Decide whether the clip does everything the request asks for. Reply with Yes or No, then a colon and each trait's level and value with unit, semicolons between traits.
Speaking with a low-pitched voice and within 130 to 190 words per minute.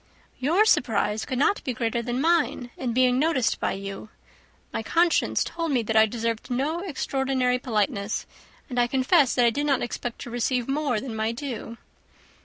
No: very high, 250 Hz; average, 180 wpm